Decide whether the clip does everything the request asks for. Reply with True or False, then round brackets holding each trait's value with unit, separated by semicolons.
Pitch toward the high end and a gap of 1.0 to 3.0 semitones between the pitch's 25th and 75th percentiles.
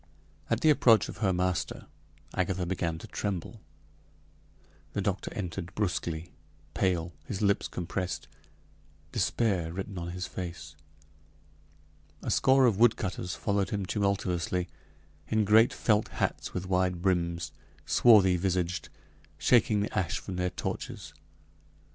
False (95 Hz; 2.7 semitones)